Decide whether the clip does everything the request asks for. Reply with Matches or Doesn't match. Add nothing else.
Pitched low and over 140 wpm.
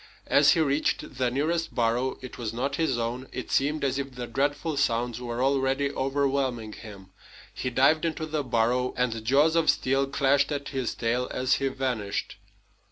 Matches